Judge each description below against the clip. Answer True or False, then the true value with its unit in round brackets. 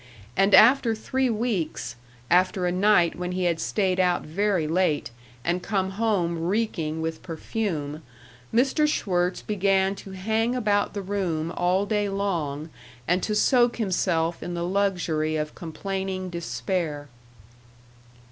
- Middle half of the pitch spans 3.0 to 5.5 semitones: True (3.5 semitones)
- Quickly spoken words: False (135 wpm)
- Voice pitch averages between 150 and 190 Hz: True (185 Hz)